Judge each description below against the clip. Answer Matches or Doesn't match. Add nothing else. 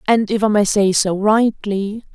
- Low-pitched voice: Doesn't match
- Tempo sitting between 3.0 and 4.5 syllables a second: Matches